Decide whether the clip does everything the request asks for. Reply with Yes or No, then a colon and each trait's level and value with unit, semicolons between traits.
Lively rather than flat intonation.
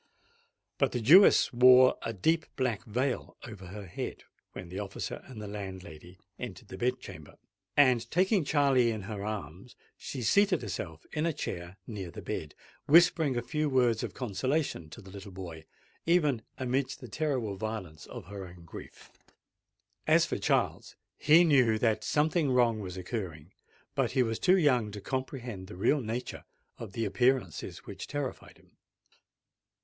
Yes: wide, 5.8 semitones